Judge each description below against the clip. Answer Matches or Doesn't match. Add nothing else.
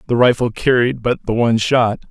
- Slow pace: Doesn't match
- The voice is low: Matches